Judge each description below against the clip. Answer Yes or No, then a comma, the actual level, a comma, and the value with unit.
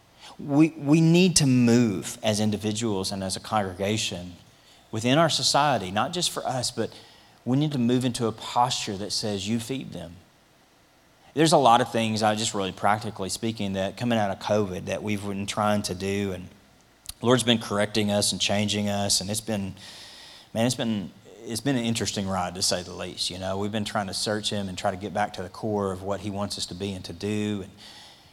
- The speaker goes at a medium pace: No, fast, 215 wpm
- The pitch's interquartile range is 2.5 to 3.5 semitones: Yes, average, 2.9 semitones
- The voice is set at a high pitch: No, low, 105 Hz